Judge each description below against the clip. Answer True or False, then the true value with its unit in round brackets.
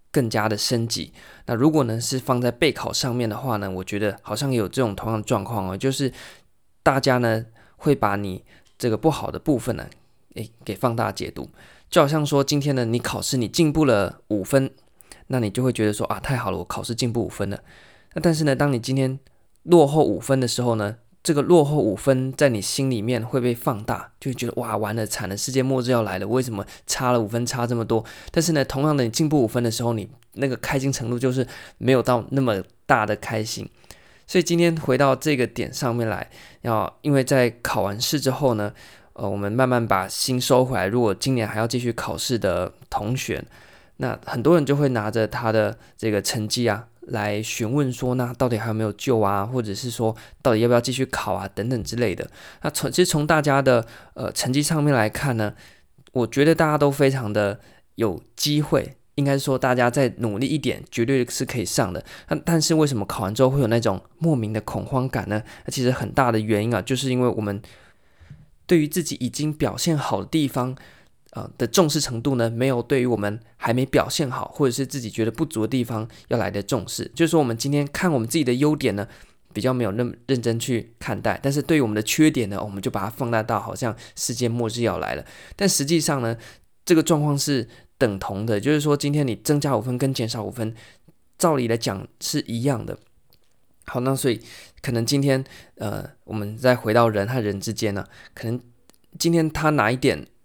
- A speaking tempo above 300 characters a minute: True (310 characters per minute)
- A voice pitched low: True (125 Hz)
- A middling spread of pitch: True (3.9 semitones)